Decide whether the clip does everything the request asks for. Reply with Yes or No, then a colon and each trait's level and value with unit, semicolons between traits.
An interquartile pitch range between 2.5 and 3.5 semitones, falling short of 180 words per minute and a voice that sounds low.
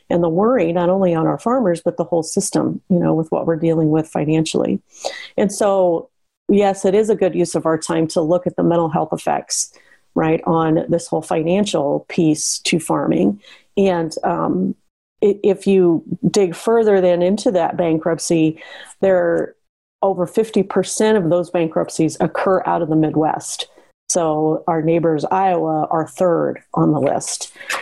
No: average, 3.0 semitones; average, 165 wpm; medium, 175 Hz